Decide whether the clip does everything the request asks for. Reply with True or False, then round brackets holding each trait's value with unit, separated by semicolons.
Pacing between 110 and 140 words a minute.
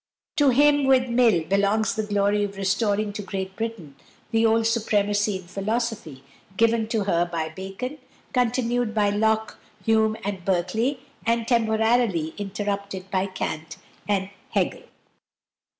True (135 wpm)